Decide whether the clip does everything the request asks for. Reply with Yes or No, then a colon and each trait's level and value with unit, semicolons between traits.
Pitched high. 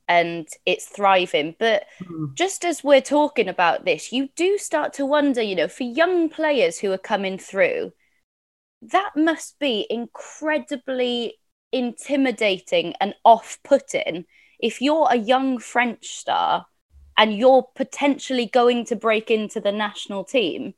Yes: very high, 250 Hz